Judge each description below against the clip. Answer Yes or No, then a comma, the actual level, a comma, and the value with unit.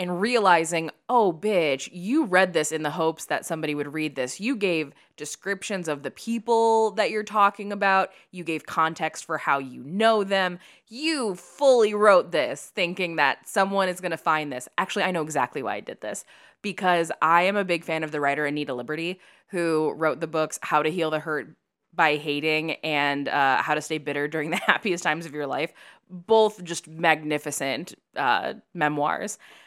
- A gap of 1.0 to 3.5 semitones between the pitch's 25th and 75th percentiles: No, average, 4.3 semitones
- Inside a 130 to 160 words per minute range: No, average, 185 wpm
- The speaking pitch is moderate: Yes, medium, 165 Hz